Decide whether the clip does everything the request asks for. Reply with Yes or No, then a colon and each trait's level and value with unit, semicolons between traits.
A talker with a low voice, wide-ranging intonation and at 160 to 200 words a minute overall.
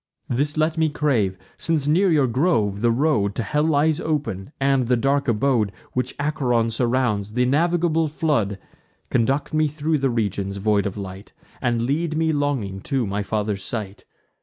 Yes: low, 130 Hz; wide, 6.1 semitones; average, 165 wpm